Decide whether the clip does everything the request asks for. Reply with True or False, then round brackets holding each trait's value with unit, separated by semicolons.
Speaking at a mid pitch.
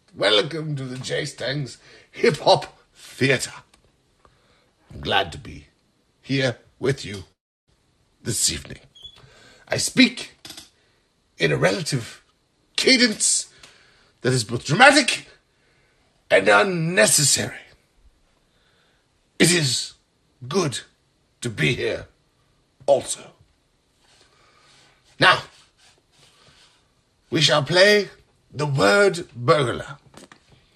True (145 Hz)